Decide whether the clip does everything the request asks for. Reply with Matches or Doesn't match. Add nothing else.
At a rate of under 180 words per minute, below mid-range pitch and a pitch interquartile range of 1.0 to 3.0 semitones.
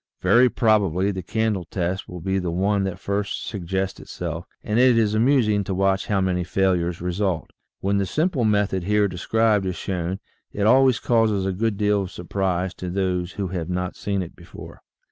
Doesn't match